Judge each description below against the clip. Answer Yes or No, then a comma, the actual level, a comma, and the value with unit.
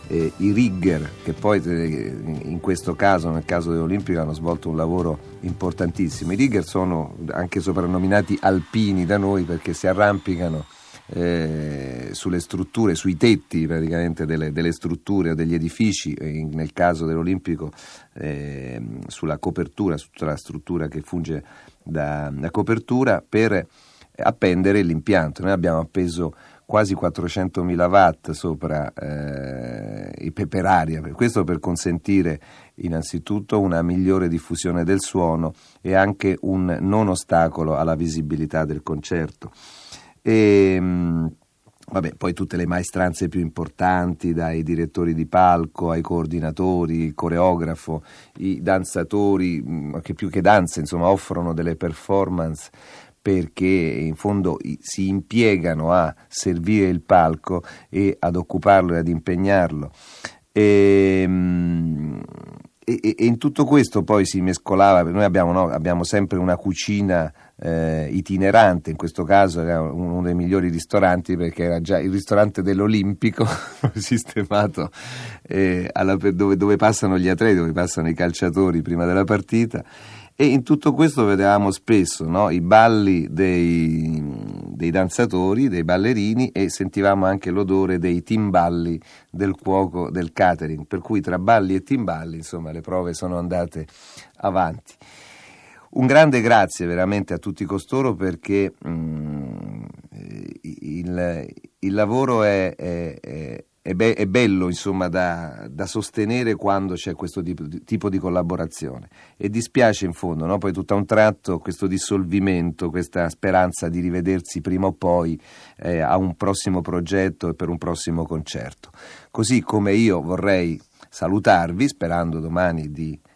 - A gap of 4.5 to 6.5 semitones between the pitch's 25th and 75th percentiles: No, average, 2.9 semitones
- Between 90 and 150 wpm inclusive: Yes, average, 135 wpm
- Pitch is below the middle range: Yes, very low, 90 Hz